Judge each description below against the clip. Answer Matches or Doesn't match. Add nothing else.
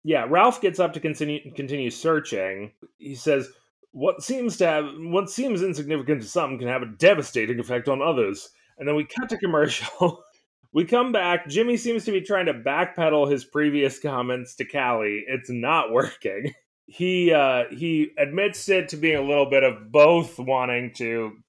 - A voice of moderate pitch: Matches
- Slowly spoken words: Doesn't match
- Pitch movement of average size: Doesn't match